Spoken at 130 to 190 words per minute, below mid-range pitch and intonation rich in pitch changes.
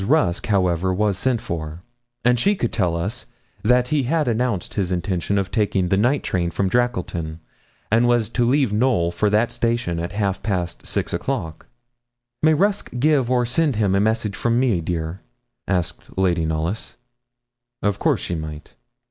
Yes: average, 170 wpm; low, 105 Hz; wide, 5.7 semitones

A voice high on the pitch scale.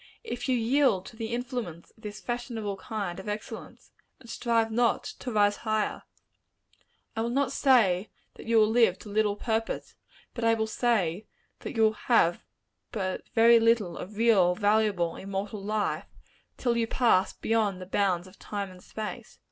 Yes: high, 220 Hz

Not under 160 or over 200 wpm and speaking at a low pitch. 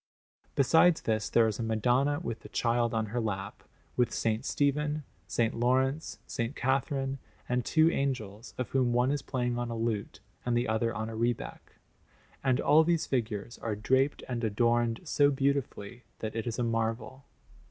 Yes: average, 175 wpm; low, 120 Hz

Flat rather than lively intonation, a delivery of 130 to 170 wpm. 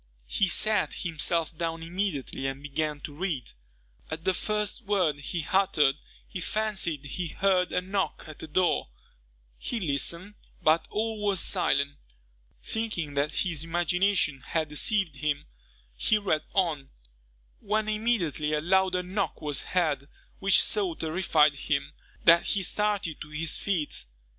No: average, 4.5 semitones; average, 140 wpm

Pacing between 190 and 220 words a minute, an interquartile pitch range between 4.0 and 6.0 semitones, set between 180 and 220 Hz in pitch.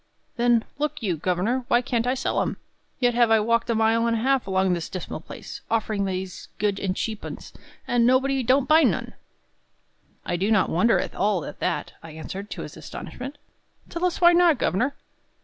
No: average, 200 wpm; average, 5.0 semitones; high, 230 Hz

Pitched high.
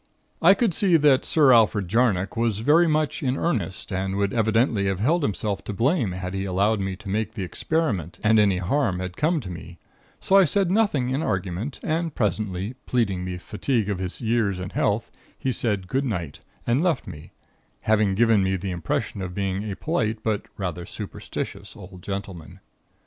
No: low, 105 Hz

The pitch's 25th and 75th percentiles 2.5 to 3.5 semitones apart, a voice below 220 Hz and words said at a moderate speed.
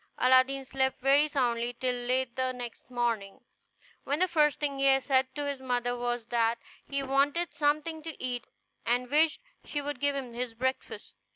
No: average, 2.8 semitones; very high, 260 Hz; average, 175 wpm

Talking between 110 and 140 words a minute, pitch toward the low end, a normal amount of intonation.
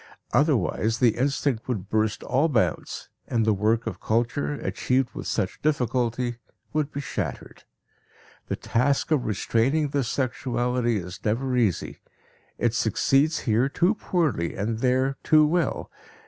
Yes: slow, 135 wpm; low, 125 Hz; average, 4.1 semitones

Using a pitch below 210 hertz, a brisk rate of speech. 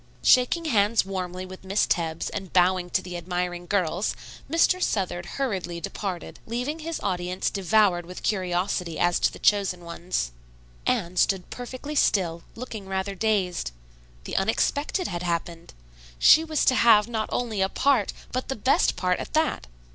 No: high, 190 Hz; average, 155 wpm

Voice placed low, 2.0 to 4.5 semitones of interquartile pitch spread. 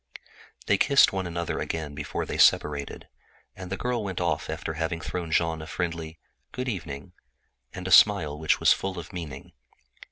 Yes: very low, 85 Hz; average, 3.1 semitones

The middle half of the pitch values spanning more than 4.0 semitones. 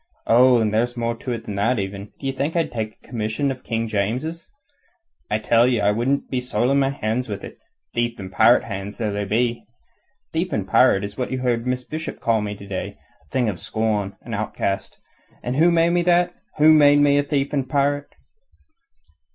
Yes: average, 4.4 semitones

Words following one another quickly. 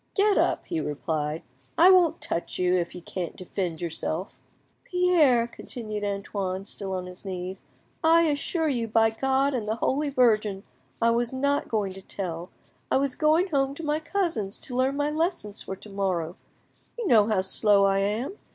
No: average, 180 wpm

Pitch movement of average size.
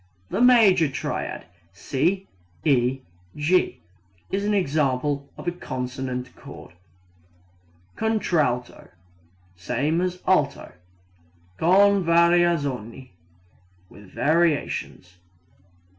No: wide, 6.0 semitones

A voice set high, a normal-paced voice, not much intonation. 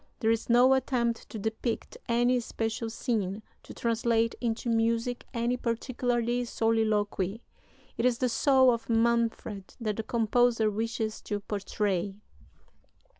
No: high, 230 Hz; slow, 125 wpm; narrow, 1.5 semitones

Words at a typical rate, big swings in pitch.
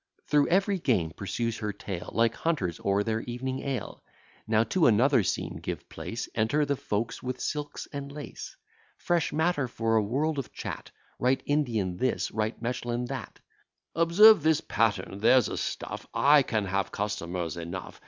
Yes: average, 165 wpm; wide, 5.7 semitones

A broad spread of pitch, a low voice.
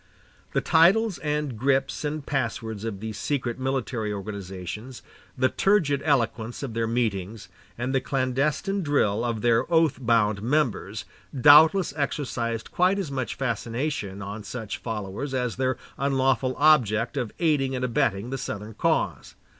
No: average, 4.4 semitones; low, 125 Hz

